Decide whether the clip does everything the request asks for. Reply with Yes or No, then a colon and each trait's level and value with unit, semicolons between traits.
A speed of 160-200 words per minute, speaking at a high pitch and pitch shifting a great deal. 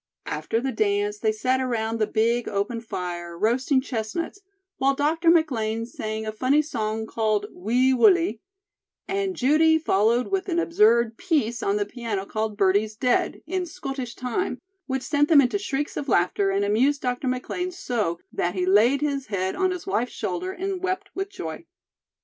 Yes: average, 170 wpm; high, 245 Hz; wide, 6.0 semitones